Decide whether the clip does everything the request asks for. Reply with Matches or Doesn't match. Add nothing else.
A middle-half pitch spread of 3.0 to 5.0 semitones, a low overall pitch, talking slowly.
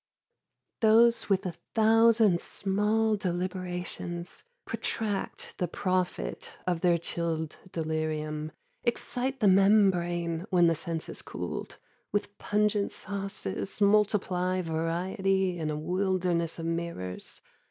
Doesn't match